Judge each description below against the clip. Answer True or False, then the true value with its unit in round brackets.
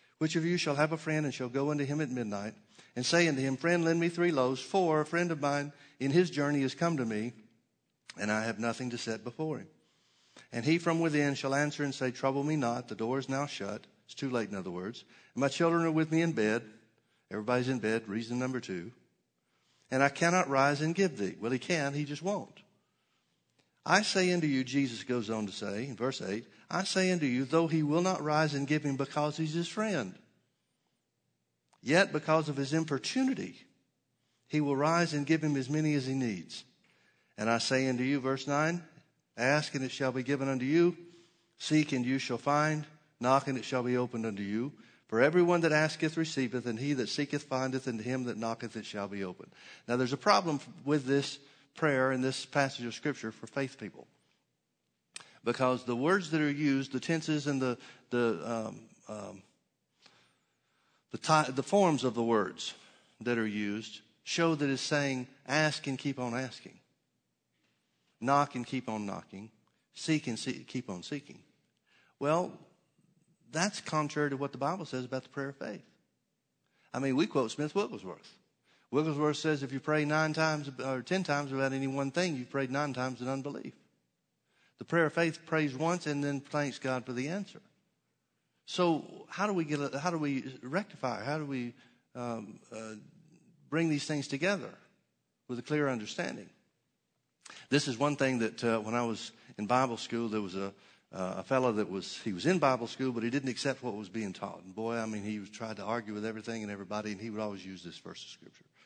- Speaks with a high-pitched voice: False (135 Hz)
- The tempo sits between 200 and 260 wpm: True (205 wpm)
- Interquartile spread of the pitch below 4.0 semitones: False (4.3 semitones)